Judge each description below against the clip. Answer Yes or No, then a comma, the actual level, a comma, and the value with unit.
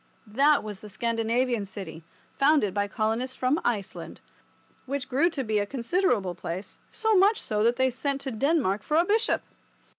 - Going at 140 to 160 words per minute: No, average, 170 wpm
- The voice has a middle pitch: No, high, 240 Hz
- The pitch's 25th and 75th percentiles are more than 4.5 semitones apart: Yes, average, 5.2 semitones